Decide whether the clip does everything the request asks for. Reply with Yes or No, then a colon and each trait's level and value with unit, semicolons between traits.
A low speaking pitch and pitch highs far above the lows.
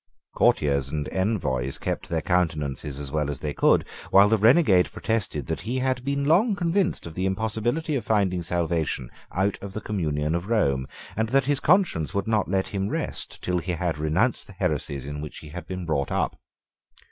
Yes: very low, 90 Hz; wide, 6.5 semitones